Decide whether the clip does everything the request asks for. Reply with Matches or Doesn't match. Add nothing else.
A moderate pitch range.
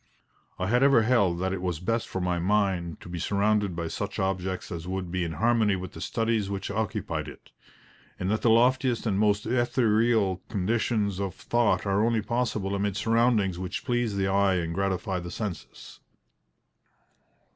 Matches